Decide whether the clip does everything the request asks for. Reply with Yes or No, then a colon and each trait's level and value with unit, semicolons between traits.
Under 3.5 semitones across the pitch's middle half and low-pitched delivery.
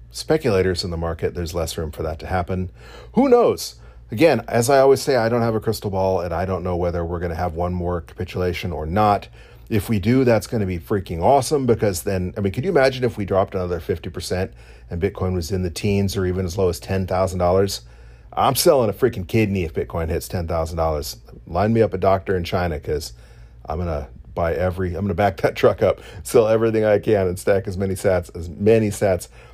Yes: average, 3.1 semitones; very low, 95 Hz